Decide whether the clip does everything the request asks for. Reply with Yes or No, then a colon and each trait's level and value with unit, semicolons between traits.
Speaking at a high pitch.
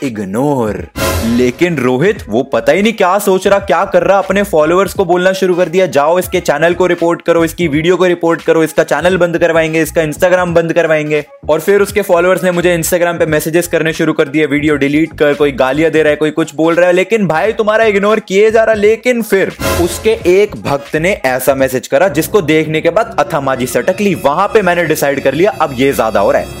No: medium, 170 Hz